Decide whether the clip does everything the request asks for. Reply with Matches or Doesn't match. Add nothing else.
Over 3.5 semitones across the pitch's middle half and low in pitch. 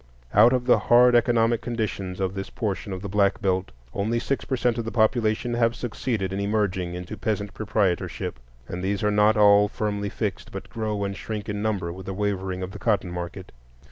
Doesn't match